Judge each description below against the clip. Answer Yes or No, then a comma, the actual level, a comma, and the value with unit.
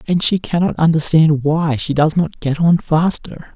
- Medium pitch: Yes, medium, 160 Hz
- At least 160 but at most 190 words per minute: No, fast, 205 wpm